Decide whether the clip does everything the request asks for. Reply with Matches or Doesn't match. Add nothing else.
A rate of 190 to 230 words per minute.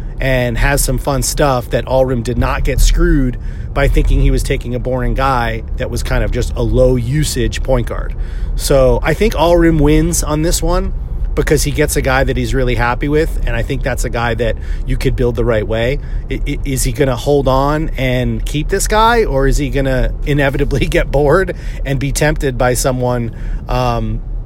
Matches